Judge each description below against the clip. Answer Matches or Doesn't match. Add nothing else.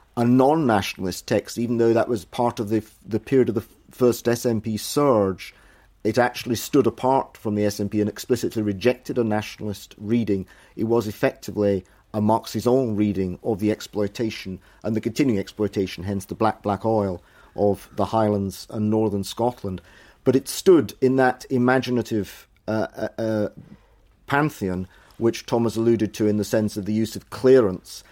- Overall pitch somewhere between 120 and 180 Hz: Doesn't match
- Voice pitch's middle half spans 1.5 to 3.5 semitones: Matches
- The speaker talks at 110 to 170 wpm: Matches